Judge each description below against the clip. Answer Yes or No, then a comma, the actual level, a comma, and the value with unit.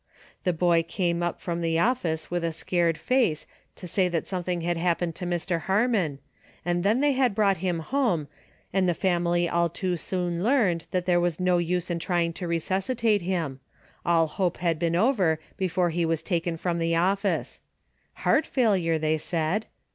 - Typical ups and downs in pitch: No, narrow, 2.2 semitones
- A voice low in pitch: No, medium, 175 Hz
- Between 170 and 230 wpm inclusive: Yes, average, 185 wpm